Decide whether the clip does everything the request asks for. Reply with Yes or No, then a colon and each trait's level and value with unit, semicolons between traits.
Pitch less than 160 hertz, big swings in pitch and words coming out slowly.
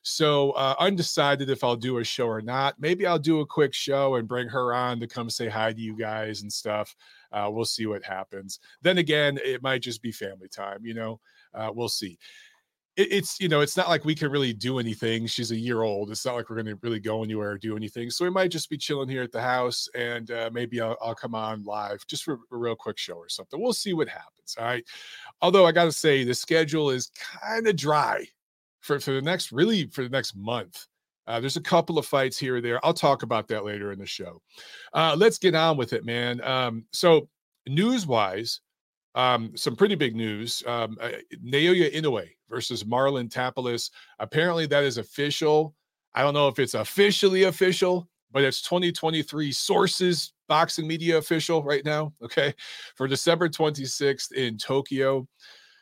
No: low, 135 Hz; wide, 5.7 semitones; fast, 205 wpm